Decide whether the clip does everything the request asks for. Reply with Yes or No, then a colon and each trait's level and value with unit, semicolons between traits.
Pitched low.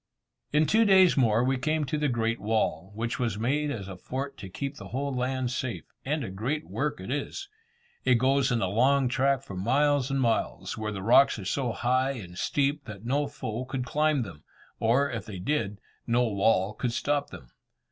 Yes: low, 125 Hz